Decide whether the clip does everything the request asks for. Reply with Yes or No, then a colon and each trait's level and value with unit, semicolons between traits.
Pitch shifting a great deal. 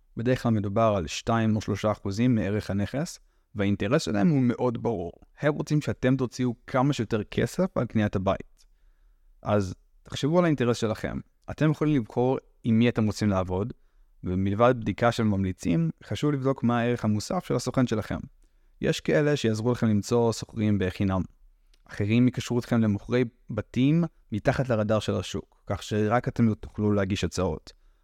No: average, 3.7 semitones